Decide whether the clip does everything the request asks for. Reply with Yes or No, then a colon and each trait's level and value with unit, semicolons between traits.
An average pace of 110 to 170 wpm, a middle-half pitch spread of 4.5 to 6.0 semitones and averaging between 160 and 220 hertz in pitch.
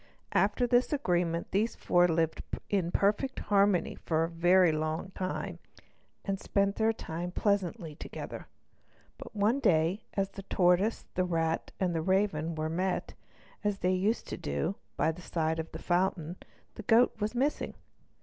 No: average, 160 wpm; average, 3.6 semitones; medium, 185 Hz